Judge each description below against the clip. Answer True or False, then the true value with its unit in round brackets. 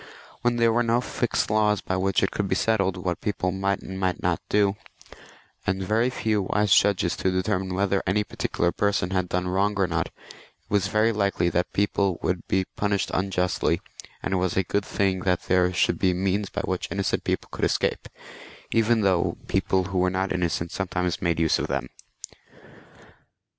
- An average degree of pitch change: False (1.9 semitones)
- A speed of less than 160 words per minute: False (190 wpm)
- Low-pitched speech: True (95 Hz)